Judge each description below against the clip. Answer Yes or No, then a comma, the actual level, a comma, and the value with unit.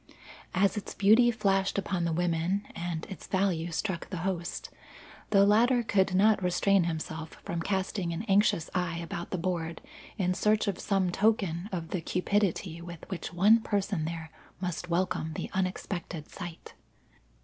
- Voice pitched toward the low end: No, medium, 185 Hz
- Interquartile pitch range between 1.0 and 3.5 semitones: Yes, average, 2.8 semitones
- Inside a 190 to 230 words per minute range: No, average, 155 wpm